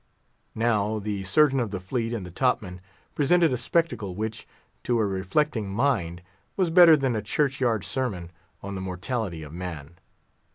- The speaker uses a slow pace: No, average, 170 wpm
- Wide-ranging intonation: Yes, wide, 5.9 semitones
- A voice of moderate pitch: No, low, 110 Hz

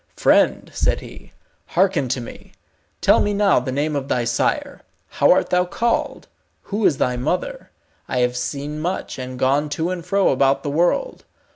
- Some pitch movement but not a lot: No, wide, 6.0 semitones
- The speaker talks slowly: No, average, 175 wpm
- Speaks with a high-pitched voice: No, medium, 150 Hz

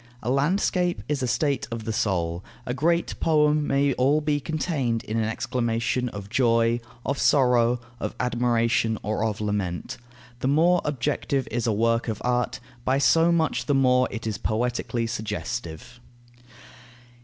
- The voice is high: No, low, 125 Hz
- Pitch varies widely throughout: No, average, 3.7 semitones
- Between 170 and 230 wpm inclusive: No, average, 155 wpm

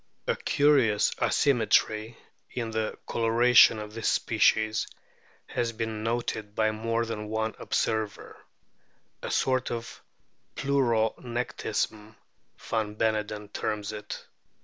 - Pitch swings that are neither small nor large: No, narrow, 1.5 semitones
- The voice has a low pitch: Yes, low, 110 Hz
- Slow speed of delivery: Yes, slow, 105 wpm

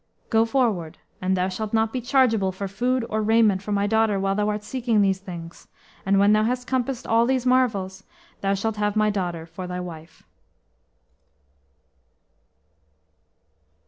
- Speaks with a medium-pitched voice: No, high, 210 Hz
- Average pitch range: Yes, average, 3.2 semitones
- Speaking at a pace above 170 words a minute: No, average, 160 wpm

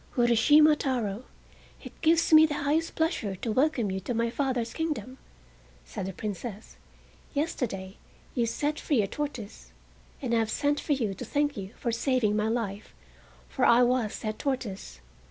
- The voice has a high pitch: Yes, high, 240 Hz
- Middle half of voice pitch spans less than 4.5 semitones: No, average, 5.3 semitones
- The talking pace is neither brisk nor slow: Yes, average, 165 wpm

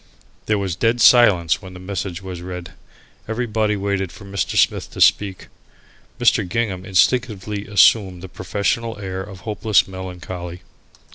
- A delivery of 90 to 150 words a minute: Yes, average, 140 wpm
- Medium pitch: No, very low, 95 Hz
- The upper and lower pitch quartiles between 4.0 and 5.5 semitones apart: No, narrow, 2.5 semitones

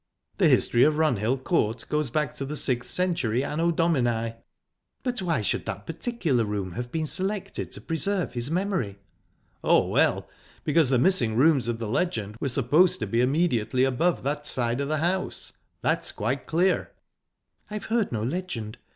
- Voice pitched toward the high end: No, medium, 140 Hz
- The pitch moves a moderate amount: No, wide, 6.4 semitones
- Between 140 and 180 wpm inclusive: Yes, average, 170 wpm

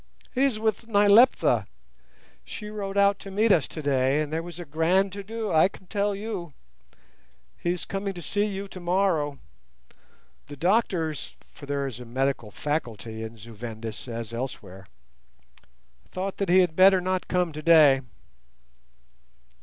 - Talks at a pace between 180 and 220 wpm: No, average, 155 wpm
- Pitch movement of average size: No, wide, 6.3 semitones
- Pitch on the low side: No, medium, 175 Hz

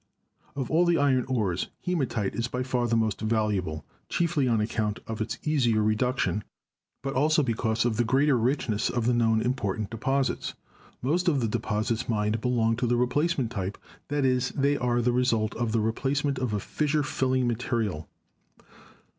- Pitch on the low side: Yes, low, 120 Hz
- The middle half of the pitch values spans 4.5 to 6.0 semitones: No, average, 3.4 semitones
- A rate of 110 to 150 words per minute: No, average, 170 wpm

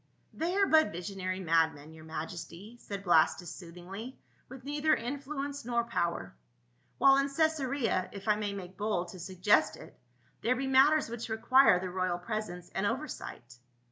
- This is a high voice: Yes, high, 205 Hz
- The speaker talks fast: No, average, 175 wpm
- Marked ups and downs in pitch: Yes, wide, 7.0 semitones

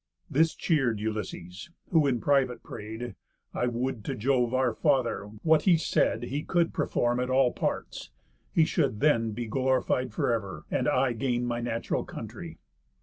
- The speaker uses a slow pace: No, average, 160 wpm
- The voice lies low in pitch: Yes, low, 125 Hz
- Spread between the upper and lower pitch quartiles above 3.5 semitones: No, average, 3.0 semitones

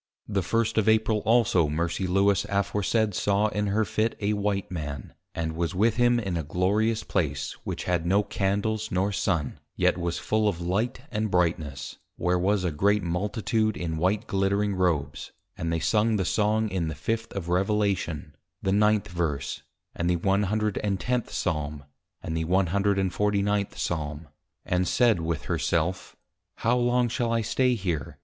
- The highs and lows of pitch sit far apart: No, average, 3.8 semitones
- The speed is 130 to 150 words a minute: No, average, 165 wpm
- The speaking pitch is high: No, low, 100 Hz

